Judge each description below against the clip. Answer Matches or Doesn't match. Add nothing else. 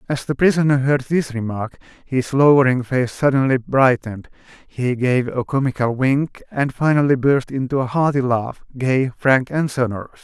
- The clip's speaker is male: Matches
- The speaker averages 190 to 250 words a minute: Doesn't match